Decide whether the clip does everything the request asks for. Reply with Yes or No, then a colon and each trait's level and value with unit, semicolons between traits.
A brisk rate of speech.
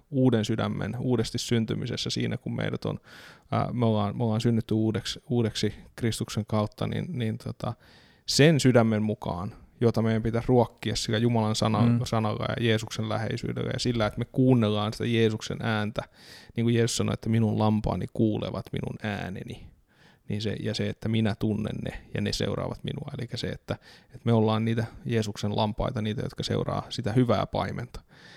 Yes: fast, 165 wpm